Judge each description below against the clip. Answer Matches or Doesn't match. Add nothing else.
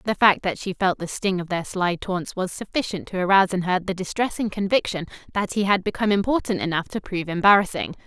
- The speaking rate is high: Matches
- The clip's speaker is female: Matches